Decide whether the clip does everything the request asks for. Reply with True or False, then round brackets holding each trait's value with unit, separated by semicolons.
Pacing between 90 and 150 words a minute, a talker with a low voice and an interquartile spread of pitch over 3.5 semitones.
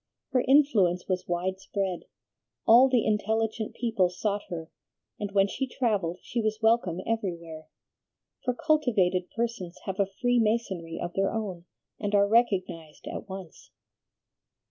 False (140 wpm; 200 Hz; 4.2 semitones)